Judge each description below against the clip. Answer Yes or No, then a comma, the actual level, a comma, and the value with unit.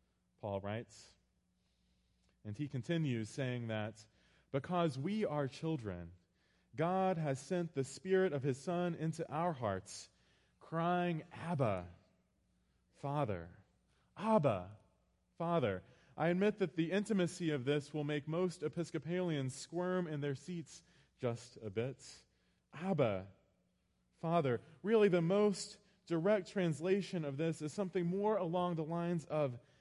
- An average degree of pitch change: No, wide, 8.5 semitones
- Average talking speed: No, slow, 125 wpm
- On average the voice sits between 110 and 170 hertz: Yes, medium, 150 Hz